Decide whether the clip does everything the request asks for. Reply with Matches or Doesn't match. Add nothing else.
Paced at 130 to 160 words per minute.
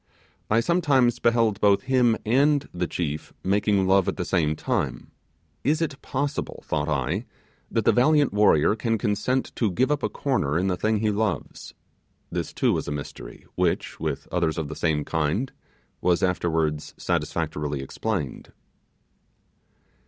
Matches